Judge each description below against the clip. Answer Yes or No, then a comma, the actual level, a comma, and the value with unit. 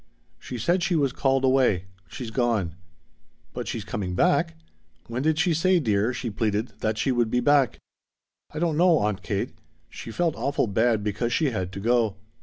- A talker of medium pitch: No, low, 120 Hz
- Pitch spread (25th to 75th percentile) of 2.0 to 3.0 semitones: No, average, 5.2 semitones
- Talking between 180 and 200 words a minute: Yes, average, 185 wpm